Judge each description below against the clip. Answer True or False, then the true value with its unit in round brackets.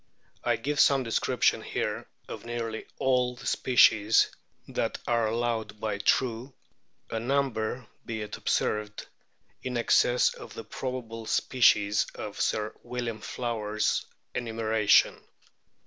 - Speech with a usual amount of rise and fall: False (2.3 semitones)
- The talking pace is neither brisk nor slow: False (115 wpm)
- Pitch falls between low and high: False (115 Hz)